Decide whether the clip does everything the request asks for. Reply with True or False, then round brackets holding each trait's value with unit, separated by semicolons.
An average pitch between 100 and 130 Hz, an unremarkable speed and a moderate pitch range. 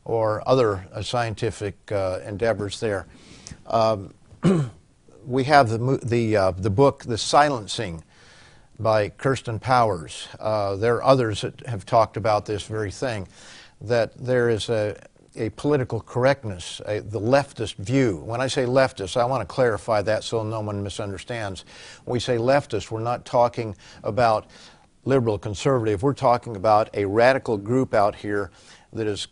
True (115 Hz; 155 wpm; 3.3 semitones)